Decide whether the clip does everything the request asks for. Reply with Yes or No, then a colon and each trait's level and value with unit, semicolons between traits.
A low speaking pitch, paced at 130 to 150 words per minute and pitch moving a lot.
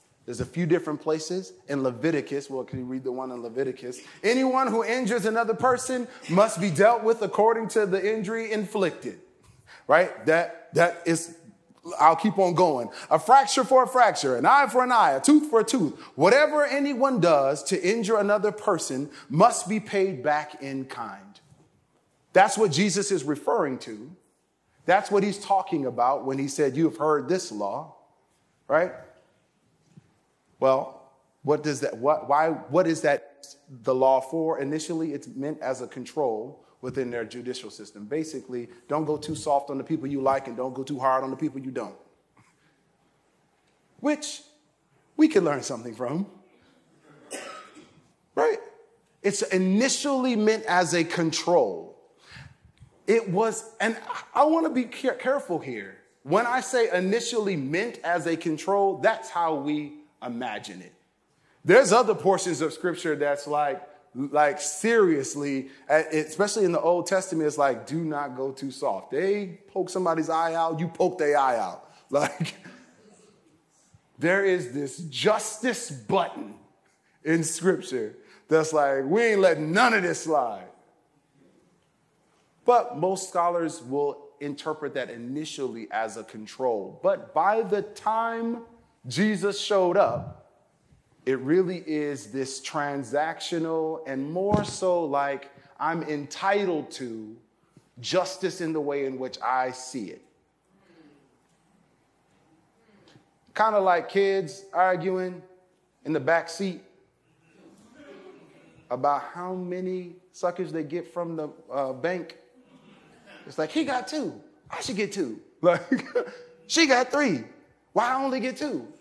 No: medium, 175 Hz; average, 145 wpm; wide, 6.9 semitones